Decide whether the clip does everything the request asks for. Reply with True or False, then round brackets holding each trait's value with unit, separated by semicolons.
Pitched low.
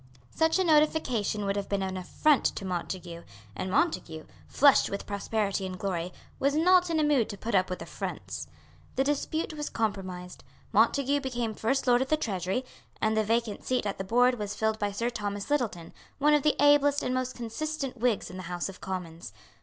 False (220 Hz)